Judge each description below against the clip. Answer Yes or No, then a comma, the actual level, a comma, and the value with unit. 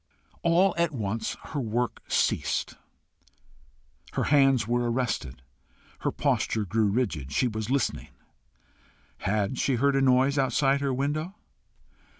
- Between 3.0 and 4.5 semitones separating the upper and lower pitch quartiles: Yes, average, 4.2 semitones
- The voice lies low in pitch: Yes, low, 130 Hz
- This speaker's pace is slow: Yes, slow, 125 wpm